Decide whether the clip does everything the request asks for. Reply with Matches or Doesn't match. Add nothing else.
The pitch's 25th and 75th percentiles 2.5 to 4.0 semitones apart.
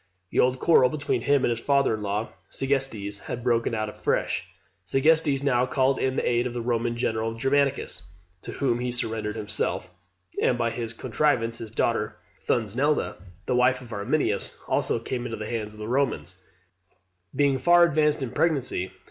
Matches